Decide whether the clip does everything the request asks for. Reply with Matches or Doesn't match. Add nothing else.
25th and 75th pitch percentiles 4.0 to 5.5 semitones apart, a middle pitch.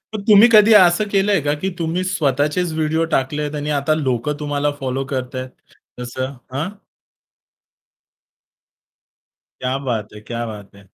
Matches